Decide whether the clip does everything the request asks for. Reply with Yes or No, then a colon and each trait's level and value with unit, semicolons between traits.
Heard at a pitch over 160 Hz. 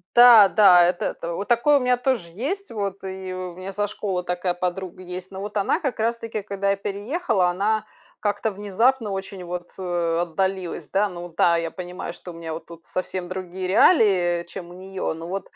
Yes: high, 190 Hz